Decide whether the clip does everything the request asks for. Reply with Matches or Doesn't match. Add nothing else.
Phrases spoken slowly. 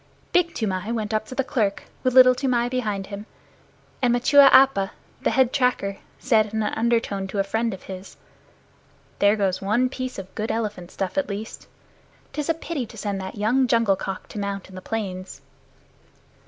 Doesn't match